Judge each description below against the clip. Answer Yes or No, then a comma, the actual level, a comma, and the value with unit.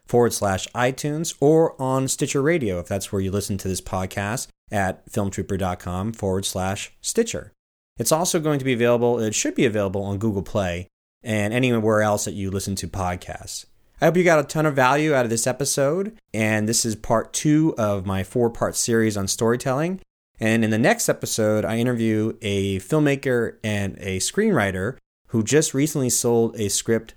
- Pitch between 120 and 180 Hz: No, low, 110 Hz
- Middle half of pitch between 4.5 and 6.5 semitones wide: Yes, average, 5.0 semitones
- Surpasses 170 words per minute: Yes, average, 185 wpm